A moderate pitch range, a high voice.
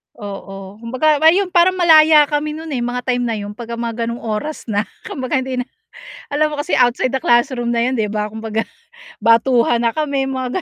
Yes: average, 4.3 semitones; high, 245 Hz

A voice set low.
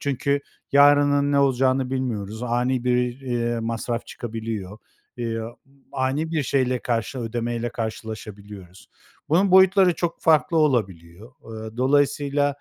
Yes: low, 125 Hz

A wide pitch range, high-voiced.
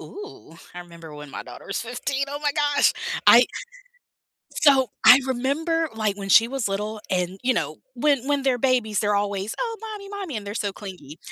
Yes: wide, 6.2 semitones; high, 245 Hz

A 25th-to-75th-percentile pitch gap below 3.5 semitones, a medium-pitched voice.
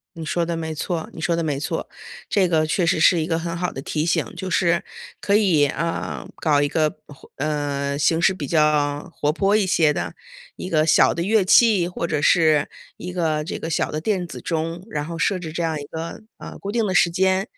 Yes: average, 2.8 semitones; medium, 165 Hz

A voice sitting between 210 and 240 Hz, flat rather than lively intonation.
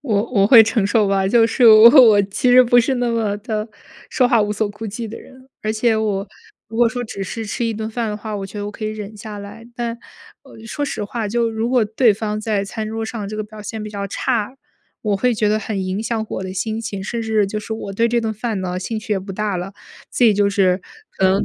Yes: high, 215 Hz; narrow, 2.1 semitones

